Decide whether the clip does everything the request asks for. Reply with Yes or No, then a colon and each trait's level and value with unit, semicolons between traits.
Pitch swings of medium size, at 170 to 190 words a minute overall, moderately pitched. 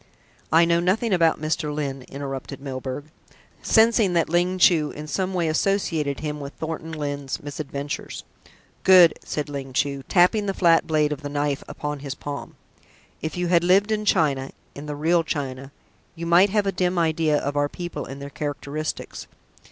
Yes: average, 3.6 semitones; average, 175 wpm; medium, 155 Hz